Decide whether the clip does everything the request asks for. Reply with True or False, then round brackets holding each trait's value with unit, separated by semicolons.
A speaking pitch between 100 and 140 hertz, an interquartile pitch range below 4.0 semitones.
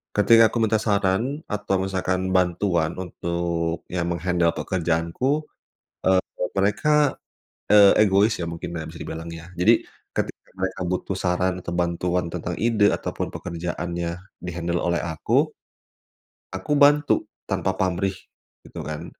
False (90 Hz; 2.8 semitones)